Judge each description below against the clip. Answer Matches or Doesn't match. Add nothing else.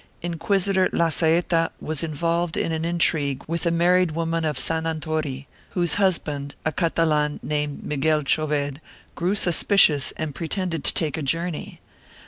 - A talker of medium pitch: Matches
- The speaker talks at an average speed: Matches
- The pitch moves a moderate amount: Doesn't match